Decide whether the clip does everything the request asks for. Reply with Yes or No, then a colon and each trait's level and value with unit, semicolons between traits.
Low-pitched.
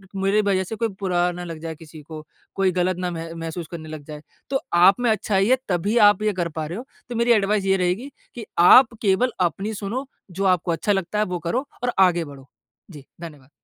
No: medium, 185 Hz